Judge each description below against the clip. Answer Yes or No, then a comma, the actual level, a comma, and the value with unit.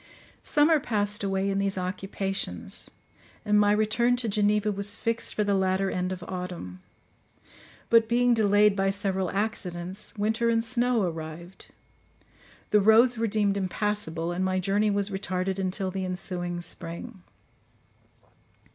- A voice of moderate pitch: No, high, 200 Hz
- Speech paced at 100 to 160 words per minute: Yes, average, 140 wpm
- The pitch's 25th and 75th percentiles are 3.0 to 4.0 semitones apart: No, narrow, 2.5 semitones